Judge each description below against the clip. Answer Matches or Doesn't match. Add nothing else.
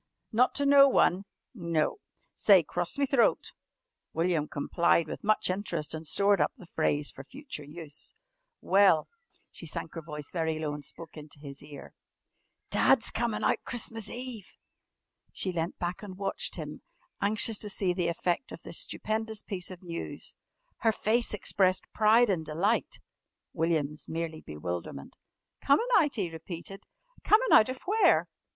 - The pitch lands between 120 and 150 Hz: Doesn't match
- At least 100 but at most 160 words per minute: Matches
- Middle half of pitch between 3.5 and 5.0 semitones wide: Doesn't match